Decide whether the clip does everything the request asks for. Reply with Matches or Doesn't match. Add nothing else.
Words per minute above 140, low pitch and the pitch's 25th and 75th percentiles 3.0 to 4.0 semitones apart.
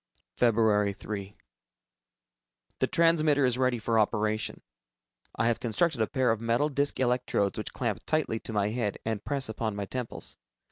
Matches